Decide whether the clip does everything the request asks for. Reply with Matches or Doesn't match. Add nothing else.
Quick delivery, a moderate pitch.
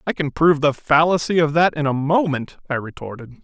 Matches